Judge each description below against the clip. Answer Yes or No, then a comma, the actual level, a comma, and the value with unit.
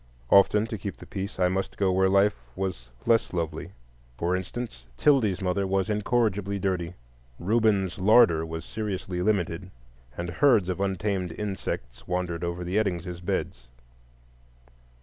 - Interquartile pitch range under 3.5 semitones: Yes, average, 2.7 semitones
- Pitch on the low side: Yes, very low, 95 Hz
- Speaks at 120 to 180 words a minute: Yes, average, 140 wpm